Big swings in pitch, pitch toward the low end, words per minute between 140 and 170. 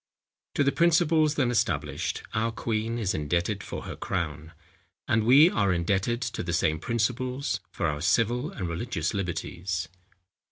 Yes: wide, 6.3 semitones; low, 110 Hz; average, 150 wpm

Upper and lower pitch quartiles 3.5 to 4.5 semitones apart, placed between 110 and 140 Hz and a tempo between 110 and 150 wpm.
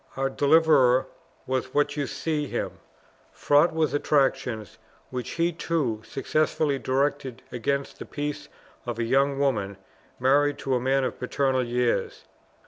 No: narrow, 2.6 semitones; low, 135 Hz; slow, 135 wpm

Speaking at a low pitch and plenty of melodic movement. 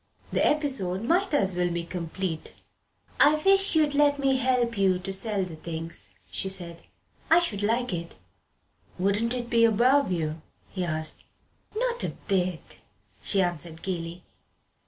No: high, 195 Hz; wide, 7.0 semitones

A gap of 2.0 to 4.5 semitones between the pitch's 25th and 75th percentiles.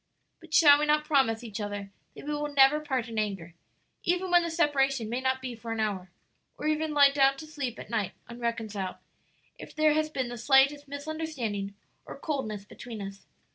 No: average, 5.3 semitones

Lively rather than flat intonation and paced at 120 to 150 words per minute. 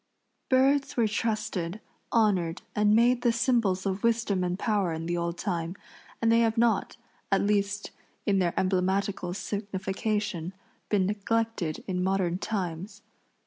No: average, 3.6 semitones; average, 140 wpm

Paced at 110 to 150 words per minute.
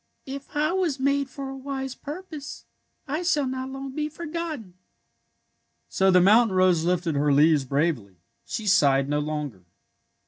No: average, 160 wpm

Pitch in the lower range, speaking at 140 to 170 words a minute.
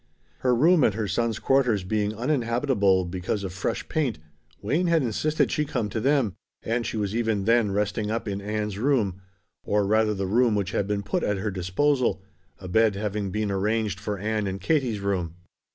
No: low, 105 Hz; average, 190 wpm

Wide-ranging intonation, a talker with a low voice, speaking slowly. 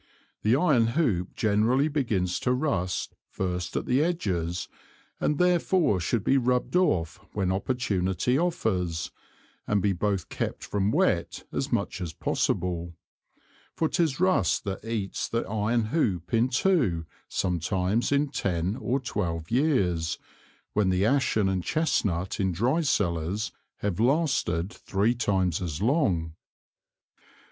Yes: wide, 6.4 semitones; low, 105 Hz; slow, 130 wpm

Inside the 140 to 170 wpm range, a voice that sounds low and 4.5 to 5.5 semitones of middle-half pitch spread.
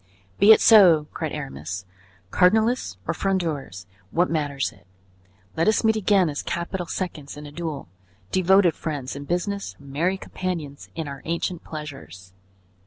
No: average, 145 wpm; medium, 160 Hz; average, 4.8 semitones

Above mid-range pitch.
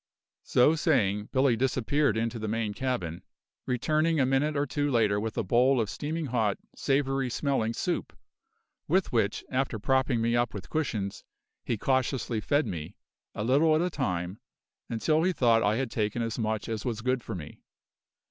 No: low, 120 Hz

